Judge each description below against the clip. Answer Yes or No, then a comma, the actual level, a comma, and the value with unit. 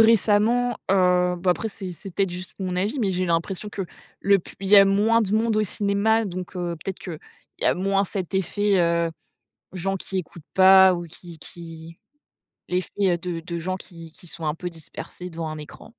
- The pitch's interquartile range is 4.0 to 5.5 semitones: No, narrow, 2.6 semitones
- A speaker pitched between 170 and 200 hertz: Yes, medium, 185 Hz